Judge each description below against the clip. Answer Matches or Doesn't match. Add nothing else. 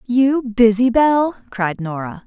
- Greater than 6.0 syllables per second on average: Doesn't match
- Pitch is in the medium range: Doesn't match